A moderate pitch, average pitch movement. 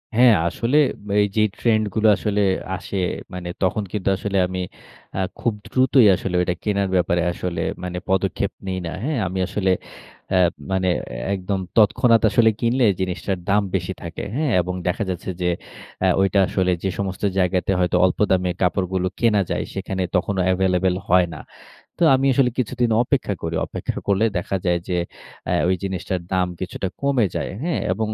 No: very low, 95 Hz; average, 3.2 semitones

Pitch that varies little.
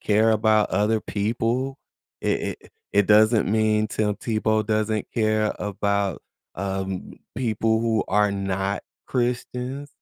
Yes: narrow, 1.7 semitones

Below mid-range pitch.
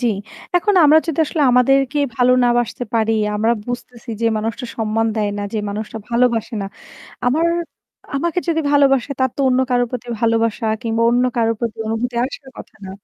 No: high, 245 Hz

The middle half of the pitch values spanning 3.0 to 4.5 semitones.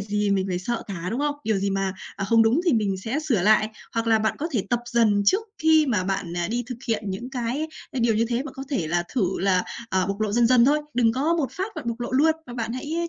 No: average, 5.0 semitones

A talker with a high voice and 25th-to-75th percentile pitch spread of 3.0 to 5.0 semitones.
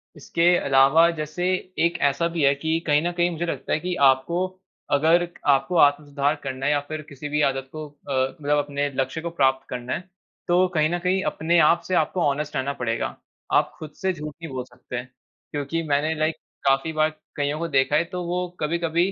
No: medium, 150 Hz; average, 3.4 semitones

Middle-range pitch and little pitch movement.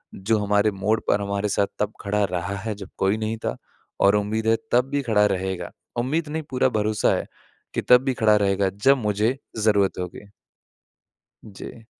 No: low, 105 Hz; narrow, 2.0 semitones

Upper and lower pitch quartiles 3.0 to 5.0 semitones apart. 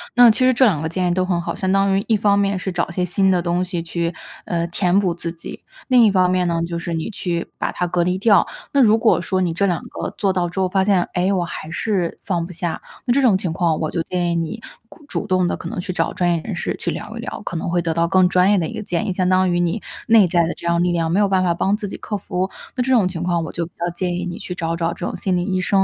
No: narrow, 2.4 semitones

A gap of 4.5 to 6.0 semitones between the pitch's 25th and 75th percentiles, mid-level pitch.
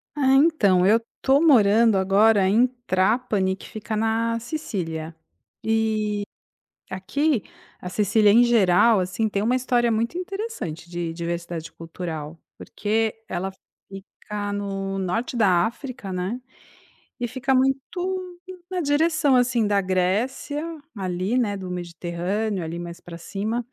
No: average, 4.9 semitones; high, 210 Hz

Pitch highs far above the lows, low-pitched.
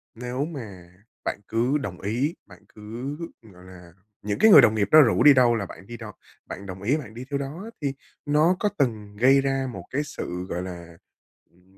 Yes: wide, 6.1 semitones; low, 115 Hz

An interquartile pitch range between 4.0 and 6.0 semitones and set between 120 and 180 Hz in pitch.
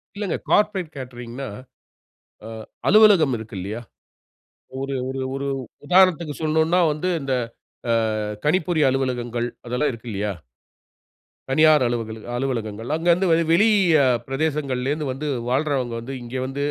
Yes: average, 4.6 semitones; low, 135 Hz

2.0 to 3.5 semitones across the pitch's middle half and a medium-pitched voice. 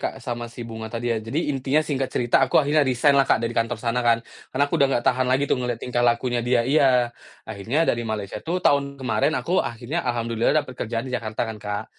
No: average, 2.9 semitones; low, 125 Hz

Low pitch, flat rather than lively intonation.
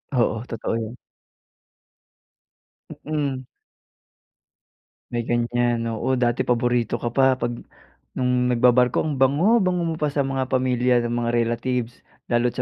Yes: low, 125 Hz; narrow, 1.9 semitones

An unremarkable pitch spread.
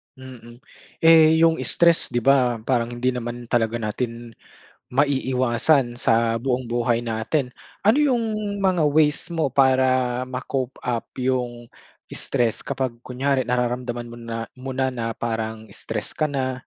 No: narrow, 2.2 semitones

